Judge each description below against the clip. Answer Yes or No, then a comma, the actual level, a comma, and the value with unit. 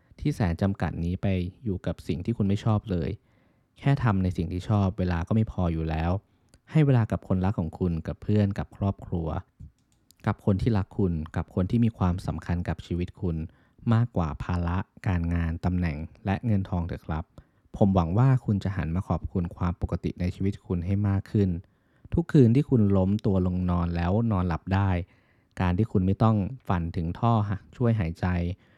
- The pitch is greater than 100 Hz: No, very low, 95 Hz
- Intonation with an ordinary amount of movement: Yes, average, 3.2 semitones